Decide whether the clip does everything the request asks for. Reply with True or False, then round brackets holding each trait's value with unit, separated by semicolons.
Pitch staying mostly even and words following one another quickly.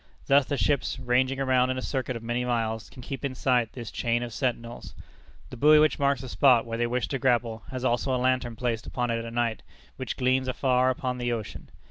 True (1.7 semitones; 225 wpm)